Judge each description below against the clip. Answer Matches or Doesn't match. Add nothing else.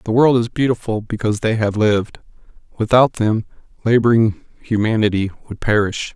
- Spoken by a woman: Doesn't match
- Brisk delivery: Doesn't match